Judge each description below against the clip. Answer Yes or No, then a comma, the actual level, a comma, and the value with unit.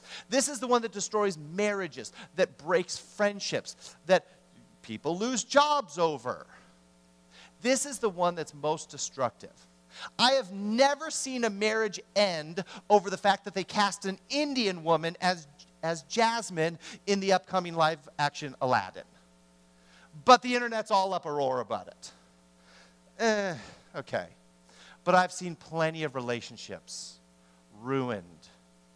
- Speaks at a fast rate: No, slow, 135 wpm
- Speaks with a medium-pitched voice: Yes, medium, 170 Hz